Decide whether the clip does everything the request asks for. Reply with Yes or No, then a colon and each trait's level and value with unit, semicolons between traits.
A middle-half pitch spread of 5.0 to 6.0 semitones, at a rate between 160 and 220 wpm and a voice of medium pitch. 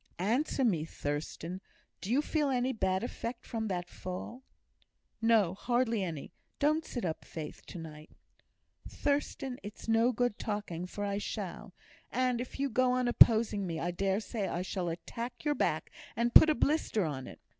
No: wide, 5.6 semitones; average, 170 wpm; high, 220 Hz